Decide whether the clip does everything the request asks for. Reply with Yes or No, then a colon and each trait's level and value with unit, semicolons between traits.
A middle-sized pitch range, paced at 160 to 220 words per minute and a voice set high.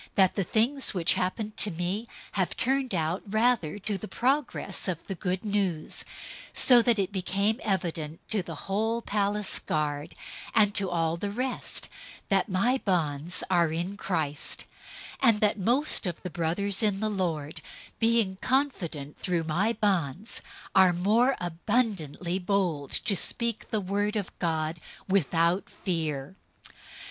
No: average, 4.2 semitones; average, 150 wpm; high, 195 Hz